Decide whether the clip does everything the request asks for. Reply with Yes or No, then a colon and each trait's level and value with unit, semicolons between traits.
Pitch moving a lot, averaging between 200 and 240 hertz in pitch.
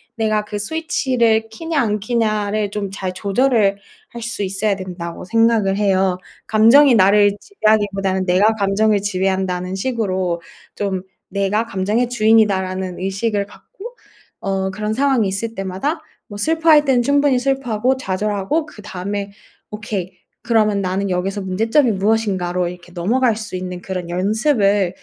No: average, 3.2 semitones; high, 205 Hz